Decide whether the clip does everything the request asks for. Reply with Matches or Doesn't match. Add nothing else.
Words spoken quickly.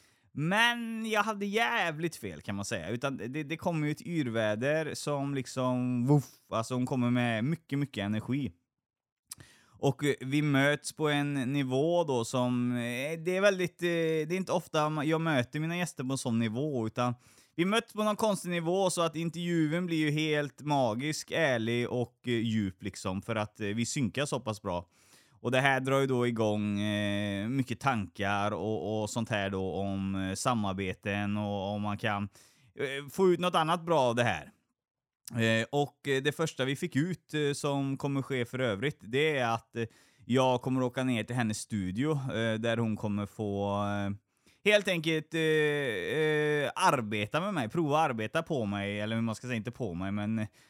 Doesn't match